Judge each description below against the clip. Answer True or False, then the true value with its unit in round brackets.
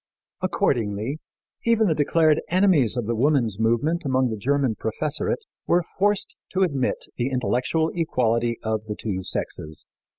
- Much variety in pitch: True (6.0 semitones)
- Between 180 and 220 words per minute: False (140 wpm)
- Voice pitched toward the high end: False (130 Hz)